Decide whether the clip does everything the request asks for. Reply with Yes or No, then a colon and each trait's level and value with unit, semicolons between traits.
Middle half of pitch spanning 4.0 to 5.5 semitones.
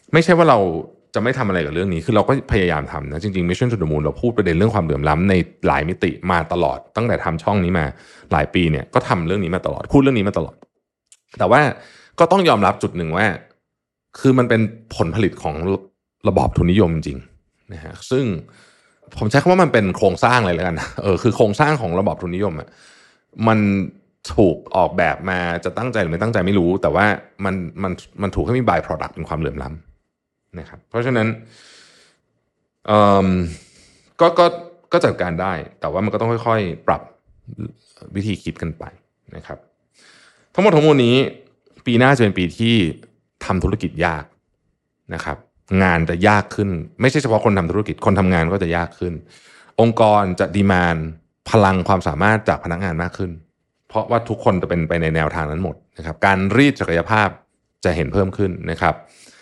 Yes: average, 4.6 semitones